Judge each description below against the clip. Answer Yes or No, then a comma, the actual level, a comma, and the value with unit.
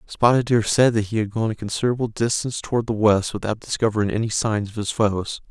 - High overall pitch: No, low, 110 Hz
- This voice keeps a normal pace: No, fast, 220 wpm